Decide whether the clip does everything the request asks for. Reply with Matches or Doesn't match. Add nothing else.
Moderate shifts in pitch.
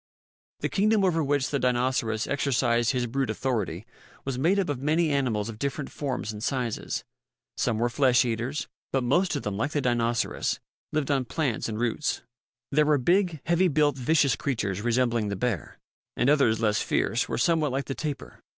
Matches